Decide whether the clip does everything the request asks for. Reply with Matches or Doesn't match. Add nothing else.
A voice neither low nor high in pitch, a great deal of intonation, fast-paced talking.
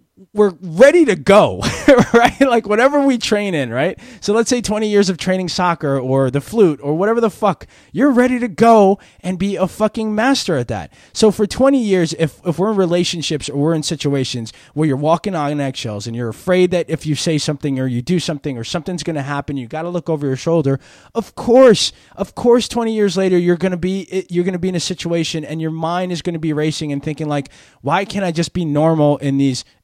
Matches